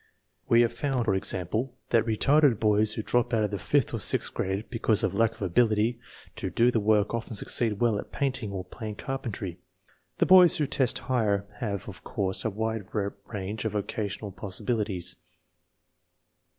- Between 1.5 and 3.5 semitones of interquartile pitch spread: Yes, average, 2.9 semitones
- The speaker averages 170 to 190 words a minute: Yes, average, 175 wpm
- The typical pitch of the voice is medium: No, low, 110 Hz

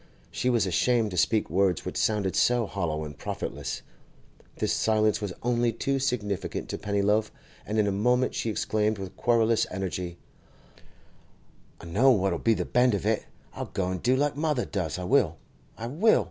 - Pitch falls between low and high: No, low, 105 Hz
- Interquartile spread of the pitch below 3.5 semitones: No, average, 4.3 semitones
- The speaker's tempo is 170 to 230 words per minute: Yes, average, 175 wpm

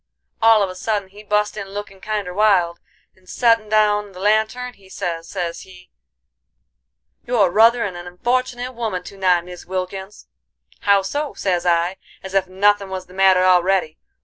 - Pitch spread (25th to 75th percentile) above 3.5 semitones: No, average, 2.7 semitones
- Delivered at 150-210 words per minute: Yes, average, 165 wpm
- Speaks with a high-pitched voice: Yes, high, 195 Hz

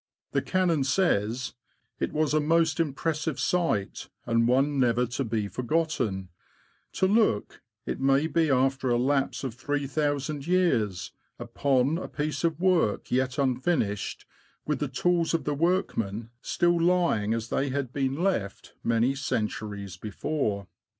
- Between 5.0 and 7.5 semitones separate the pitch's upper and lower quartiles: Yes, wide, 5.5 semitones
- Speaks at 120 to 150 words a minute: Yes, average, 140 wpm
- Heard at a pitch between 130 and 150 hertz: Yes, low, 135 Hz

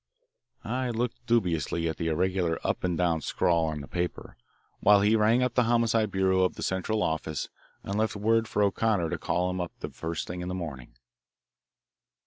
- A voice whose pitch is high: No, very low, 95 Hz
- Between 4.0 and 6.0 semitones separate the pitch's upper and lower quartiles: Yes, average, 4.7 semitones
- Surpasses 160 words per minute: Yes, average, 190 wpm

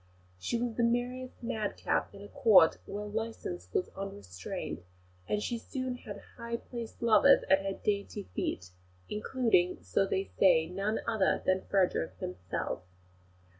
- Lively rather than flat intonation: No, average, 4.2 semitones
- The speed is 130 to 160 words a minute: Yes, average, 140 wpm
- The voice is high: Yes, high, 205 Hz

